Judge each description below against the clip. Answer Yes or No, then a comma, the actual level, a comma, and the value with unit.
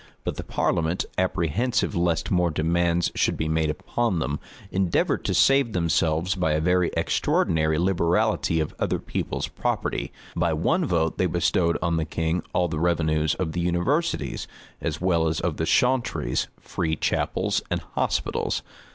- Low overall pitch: Yes, very low, 85 Hz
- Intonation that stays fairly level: Yes, narrow, 2.2 semitones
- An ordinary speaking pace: Yes, average, 155 wpm